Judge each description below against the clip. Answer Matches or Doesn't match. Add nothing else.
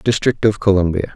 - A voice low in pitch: Matches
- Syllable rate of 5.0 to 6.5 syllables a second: Matches